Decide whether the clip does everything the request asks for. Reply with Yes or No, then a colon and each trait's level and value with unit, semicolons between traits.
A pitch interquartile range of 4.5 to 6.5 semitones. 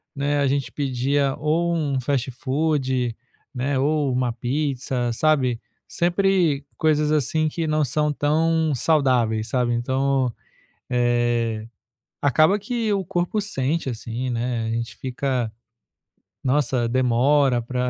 No: average, 3.8 semitones